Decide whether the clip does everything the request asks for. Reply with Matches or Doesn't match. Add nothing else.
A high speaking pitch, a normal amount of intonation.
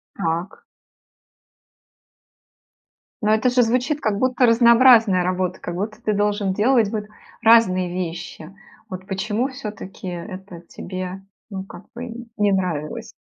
Matches